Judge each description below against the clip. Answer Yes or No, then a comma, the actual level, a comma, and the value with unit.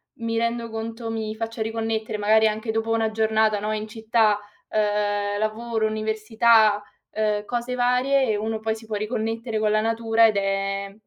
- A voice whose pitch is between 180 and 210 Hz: No, high, 220 Hz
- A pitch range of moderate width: No, narrow, 1.0 semitones